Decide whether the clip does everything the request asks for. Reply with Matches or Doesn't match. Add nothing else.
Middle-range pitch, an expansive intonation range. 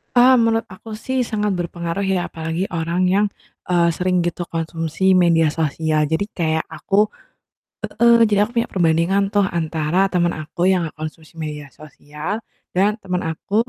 Doesn't match